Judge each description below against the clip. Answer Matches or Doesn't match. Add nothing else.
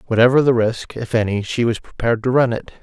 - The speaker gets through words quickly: Matches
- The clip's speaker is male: Matches